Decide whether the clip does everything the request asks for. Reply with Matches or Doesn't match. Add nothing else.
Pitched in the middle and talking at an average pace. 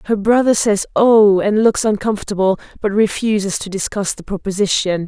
Doesn't match